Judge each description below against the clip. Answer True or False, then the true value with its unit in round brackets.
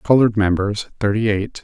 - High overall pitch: False (105 Hz)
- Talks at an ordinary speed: True (145 wpm)